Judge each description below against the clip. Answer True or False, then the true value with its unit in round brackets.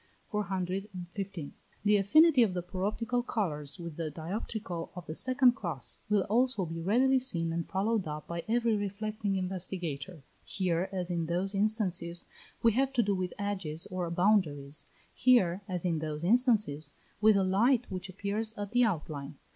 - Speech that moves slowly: False (160 wpm)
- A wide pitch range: False (4.1 semitones)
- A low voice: False (190 Hz)